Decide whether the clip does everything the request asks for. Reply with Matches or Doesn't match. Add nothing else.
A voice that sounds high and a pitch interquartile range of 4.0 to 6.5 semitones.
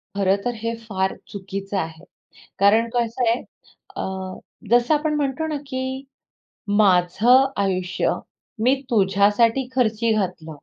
Matches